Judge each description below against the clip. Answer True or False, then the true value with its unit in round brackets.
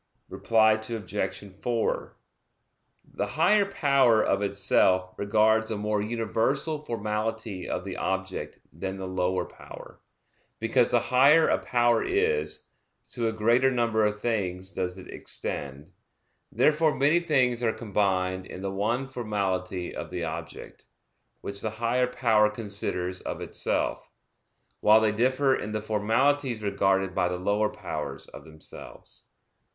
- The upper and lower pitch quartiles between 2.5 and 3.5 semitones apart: False (4.0 semitones)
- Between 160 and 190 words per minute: False (135 wpm)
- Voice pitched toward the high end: False (110 Hz)